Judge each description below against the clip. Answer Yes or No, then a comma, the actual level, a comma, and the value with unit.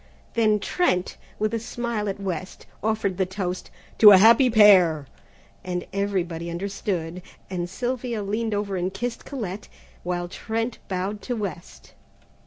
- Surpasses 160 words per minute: No, average, 140 wpm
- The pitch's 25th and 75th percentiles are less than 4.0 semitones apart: Yes, average, 3.3 semitones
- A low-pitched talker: No, high, 200 Hz